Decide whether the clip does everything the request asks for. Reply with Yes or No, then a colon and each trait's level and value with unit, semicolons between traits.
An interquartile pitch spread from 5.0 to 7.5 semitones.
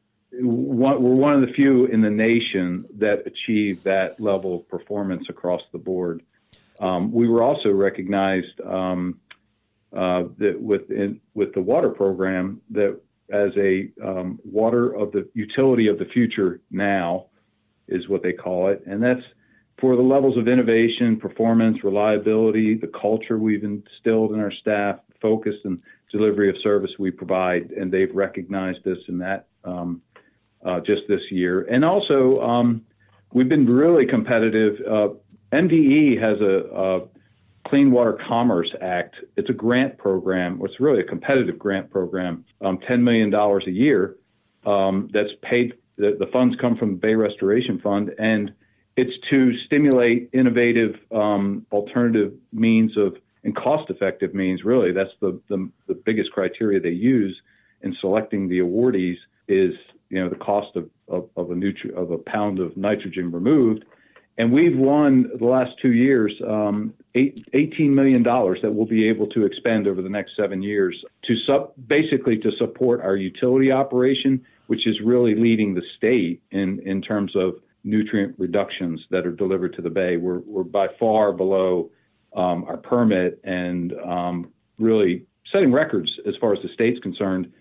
No: average, 3.9 semitones